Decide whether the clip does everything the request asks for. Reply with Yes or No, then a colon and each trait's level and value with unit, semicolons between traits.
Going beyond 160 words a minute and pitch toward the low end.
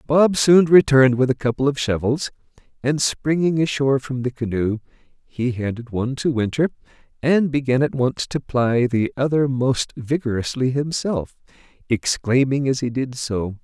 No: average, 155 wpm; low, 130 Hz